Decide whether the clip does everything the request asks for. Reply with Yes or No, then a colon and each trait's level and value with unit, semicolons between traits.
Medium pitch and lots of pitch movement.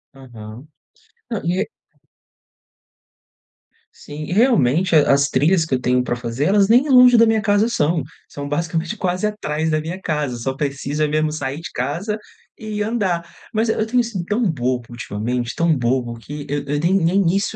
Yes: medium, 160 Hz; wide, 7.0 semitones